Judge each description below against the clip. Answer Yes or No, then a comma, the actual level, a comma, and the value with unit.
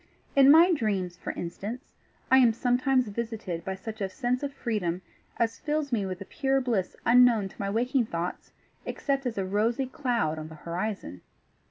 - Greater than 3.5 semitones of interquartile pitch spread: Yes, average, 5.1 semitones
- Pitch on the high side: Yes, high, 225 Hz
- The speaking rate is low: No, average, 180 wpm